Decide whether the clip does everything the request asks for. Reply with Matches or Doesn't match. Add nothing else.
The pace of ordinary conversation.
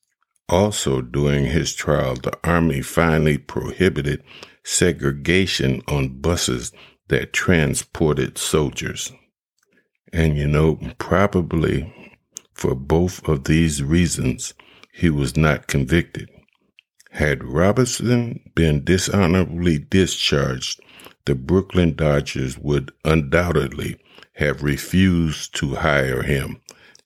Doesn't match